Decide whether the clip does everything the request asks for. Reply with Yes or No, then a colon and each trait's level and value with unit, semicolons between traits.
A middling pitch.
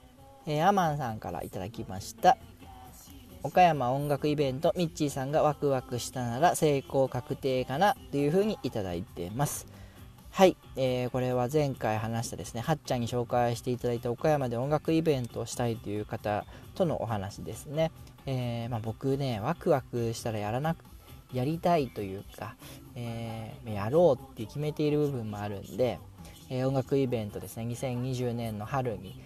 No: low, 125 Hz